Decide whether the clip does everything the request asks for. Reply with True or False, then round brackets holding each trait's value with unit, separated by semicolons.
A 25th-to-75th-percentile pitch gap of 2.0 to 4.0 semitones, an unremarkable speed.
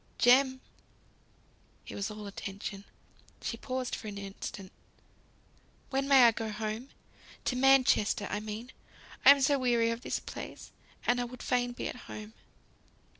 True (3.3 semitones; 150 wpm)